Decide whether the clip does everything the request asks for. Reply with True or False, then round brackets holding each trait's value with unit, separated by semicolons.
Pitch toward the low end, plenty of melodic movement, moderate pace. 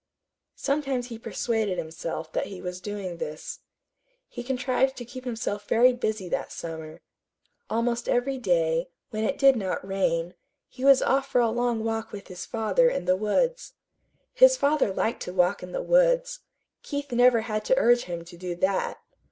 False (225 Hz; 6.0 semitones; 175 wpm)